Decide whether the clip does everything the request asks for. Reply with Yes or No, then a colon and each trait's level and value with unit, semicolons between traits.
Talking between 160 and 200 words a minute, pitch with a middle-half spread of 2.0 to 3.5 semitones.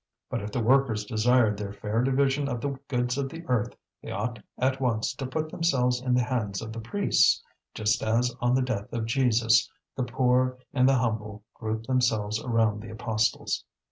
Yes: average, 190 wpm; average, 2.8 semitones